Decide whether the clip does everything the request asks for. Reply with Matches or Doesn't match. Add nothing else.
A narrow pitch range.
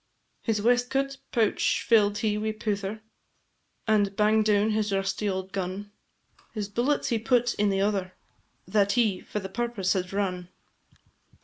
Matches